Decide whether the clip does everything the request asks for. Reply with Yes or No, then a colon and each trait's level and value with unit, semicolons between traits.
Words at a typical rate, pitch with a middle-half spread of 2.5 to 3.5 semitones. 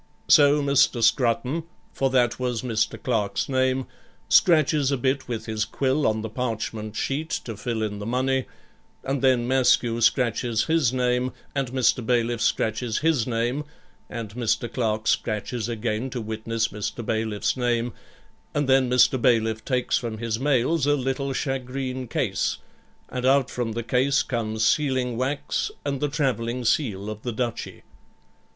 Yes: average, 155 wpm; average, 2.9 semitones